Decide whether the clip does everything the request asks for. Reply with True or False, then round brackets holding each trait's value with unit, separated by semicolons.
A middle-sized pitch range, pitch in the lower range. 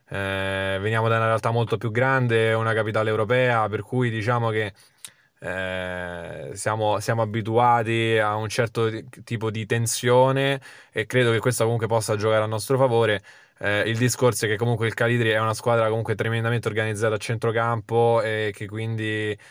False (1.4 semitones; 115 Hz)